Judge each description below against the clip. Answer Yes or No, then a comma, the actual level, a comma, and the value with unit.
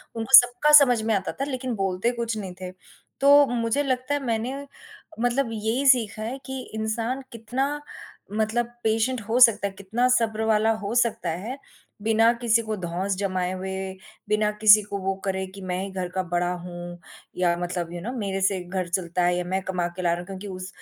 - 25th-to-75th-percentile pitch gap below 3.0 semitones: No, average, 4.1 semitones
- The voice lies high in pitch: Yes, high, 215 Hz